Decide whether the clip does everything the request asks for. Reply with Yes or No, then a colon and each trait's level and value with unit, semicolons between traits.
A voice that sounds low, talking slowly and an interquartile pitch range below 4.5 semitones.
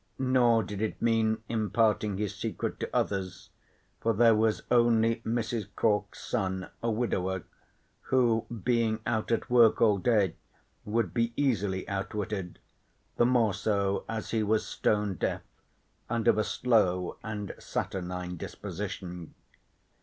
Yes: low, 110 Hz; slow, 130 wpm; average, 2.9 semitones